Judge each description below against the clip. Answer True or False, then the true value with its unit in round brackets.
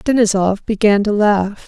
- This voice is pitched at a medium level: False (205 Hz)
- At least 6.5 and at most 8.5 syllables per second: False (4.5 syllables/s)